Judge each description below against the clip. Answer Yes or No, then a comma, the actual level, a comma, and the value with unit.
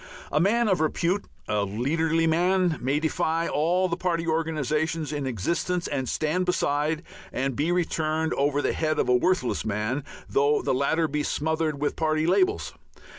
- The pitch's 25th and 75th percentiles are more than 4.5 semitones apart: No, average, 2.8 semitones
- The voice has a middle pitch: Yes, medium, 155 Hz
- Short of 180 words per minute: Yes, average, 165 wpm